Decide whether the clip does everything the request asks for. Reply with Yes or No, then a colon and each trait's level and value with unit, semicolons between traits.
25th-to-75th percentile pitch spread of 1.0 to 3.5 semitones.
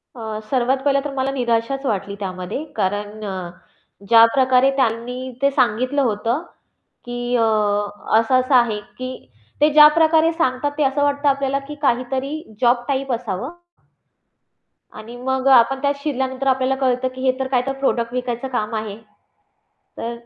Yes: average, 2.7 semitones